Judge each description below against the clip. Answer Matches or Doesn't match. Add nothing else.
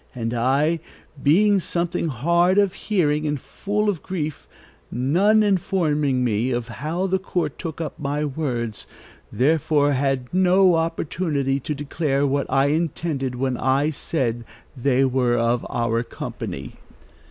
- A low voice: Doesn't match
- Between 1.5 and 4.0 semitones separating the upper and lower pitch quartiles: Doesn't match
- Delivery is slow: Matches